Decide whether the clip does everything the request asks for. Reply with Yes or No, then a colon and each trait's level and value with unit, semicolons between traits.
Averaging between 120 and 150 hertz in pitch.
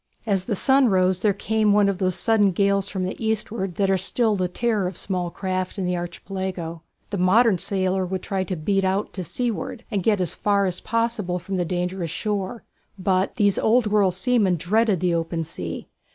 No: high, 190 Hz